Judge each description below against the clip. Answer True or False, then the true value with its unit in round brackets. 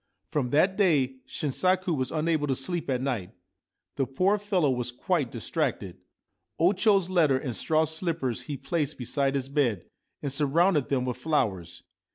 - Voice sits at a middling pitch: True (145 Hz)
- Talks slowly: False (160 wpm)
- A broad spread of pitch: False (4.8 semitones)